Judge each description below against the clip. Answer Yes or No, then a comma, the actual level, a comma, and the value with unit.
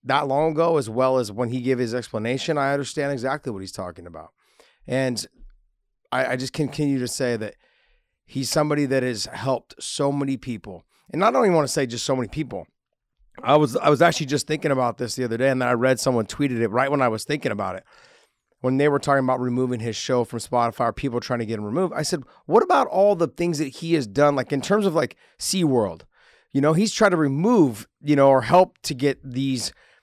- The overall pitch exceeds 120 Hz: Yes, low, 135 Hz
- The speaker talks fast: Yes, fast, 235 wpm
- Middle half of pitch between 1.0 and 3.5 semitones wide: Yes, average, 3.2 semitones